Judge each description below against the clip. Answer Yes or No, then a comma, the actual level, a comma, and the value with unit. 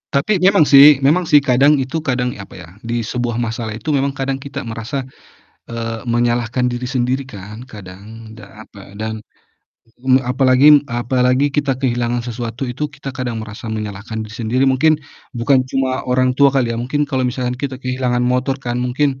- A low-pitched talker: Yes, low, 125 Hz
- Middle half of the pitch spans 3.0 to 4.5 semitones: No, narrow, 2.4 semitones